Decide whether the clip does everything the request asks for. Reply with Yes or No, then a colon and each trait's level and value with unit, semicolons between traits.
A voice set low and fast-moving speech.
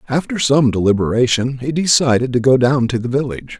No: low, 130 Hz; average, 185 wpm